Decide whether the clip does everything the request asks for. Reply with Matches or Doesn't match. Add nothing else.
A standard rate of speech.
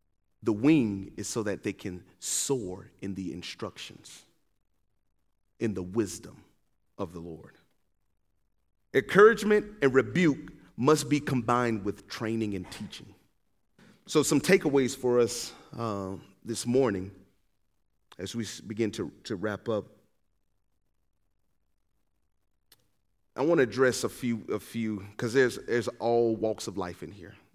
Doesn't match